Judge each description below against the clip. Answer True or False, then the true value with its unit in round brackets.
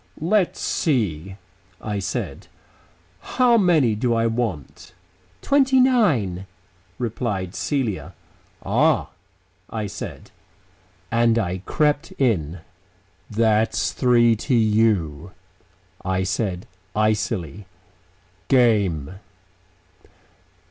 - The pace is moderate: False (80 wpm)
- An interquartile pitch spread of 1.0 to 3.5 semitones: False (5.1 semitones)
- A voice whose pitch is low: True (110 Hz)